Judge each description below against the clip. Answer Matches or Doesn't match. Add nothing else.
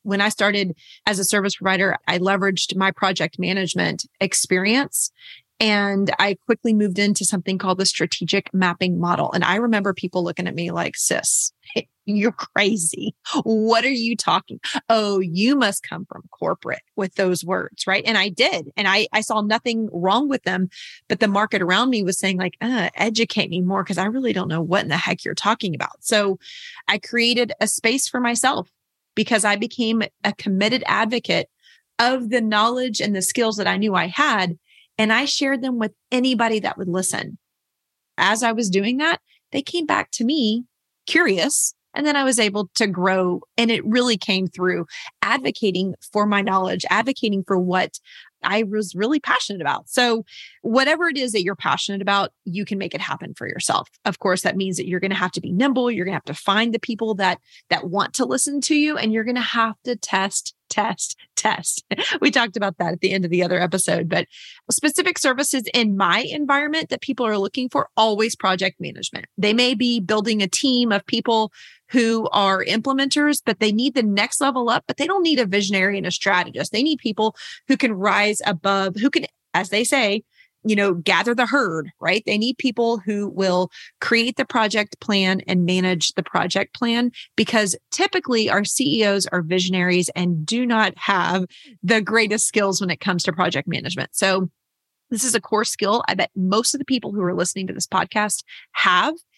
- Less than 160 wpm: Doesn't match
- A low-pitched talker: Doesn't match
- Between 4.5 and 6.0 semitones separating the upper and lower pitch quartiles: Doesn't match